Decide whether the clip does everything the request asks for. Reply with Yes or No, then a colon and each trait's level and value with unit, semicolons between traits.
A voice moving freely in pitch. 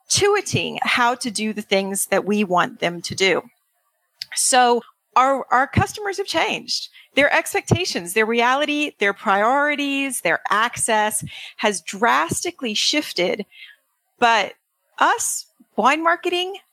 Yes: wide, 7.0 semitones